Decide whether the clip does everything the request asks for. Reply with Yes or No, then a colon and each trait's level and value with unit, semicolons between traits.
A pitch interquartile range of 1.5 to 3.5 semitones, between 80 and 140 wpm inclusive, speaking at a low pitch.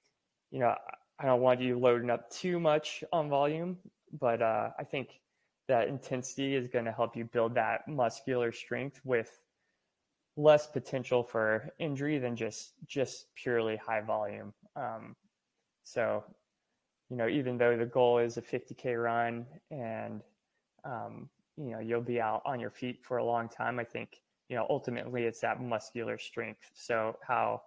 No: average, 2.7 semitones; average, 165 wpm; low, 125 Hz